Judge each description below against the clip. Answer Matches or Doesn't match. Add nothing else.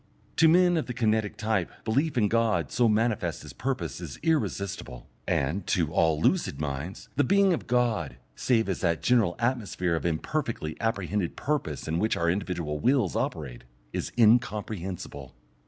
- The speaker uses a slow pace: Doesn't match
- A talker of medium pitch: Doesn't match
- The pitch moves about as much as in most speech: Doesn't match